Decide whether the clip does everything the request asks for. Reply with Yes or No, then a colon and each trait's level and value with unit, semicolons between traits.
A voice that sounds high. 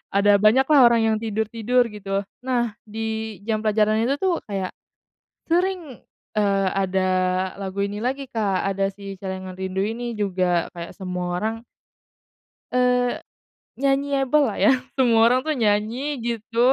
Yes: high, 220 Hz